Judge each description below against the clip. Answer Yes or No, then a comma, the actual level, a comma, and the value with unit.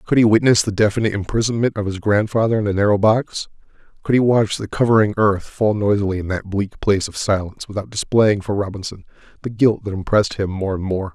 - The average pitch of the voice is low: Yes, low, 105 Hz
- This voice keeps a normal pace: No, fast, 210 wpm